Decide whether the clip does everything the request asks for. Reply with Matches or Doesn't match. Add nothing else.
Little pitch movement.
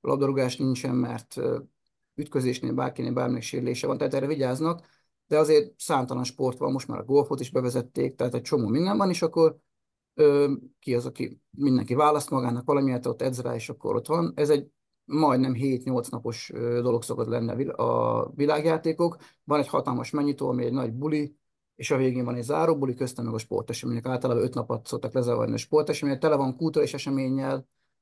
Doesn't match